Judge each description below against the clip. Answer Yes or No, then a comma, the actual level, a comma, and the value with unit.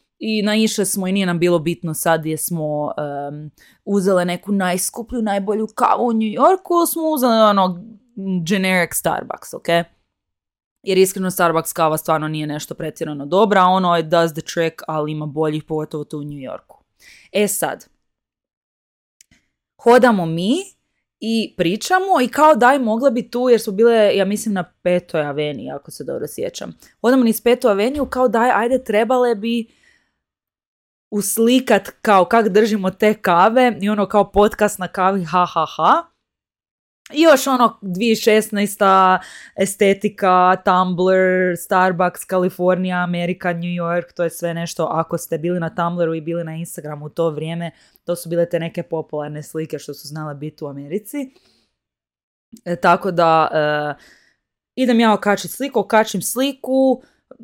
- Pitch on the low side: No, medium, 185 Hz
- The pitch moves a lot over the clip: No, average, 4.7 semitones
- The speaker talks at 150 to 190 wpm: Yes, average, 155 wpm